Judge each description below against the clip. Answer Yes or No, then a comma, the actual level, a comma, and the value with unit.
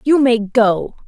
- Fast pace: No, average, 165 wpm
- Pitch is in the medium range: No, high, 235 Hz